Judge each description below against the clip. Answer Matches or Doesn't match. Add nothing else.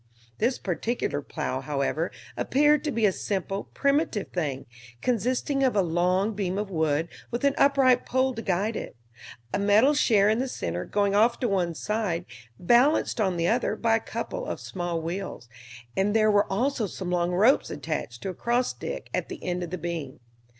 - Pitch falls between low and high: Doesn't match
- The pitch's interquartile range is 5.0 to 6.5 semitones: Matches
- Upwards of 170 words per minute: Matches